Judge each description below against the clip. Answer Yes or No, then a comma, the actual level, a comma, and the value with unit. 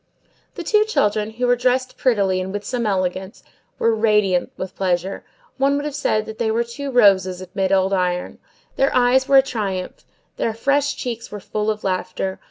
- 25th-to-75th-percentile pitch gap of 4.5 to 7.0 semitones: Yes, average, 4.9 semitones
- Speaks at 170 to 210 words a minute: Yes, average, 185 wpm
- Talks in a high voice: Yes, high, 215 Hz